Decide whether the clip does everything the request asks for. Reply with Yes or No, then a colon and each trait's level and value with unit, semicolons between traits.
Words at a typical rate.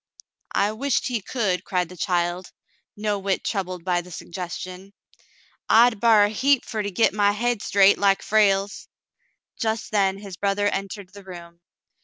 Yes: average, 165 wpm